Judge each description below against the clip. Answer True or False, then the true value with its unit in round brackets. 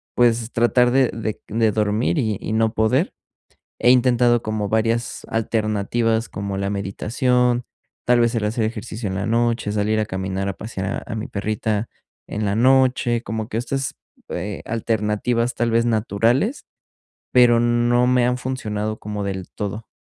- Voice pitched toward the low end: True (115 Hz)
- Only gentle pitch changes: True (2.3 semitones)